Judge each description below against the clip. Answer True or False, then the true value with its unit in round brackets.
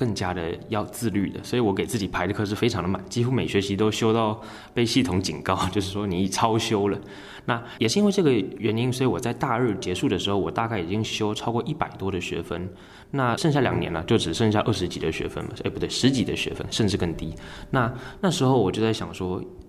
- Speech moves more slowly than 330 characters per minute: False (345 characters per minute)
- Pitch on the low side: True (105 Hz)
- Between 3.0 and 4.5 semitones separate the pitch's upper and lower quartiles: True (4.0 semitones)